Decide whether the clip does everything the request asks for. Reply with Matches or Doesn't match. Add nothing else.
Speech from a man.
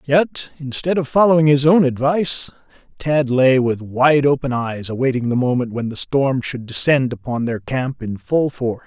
Matches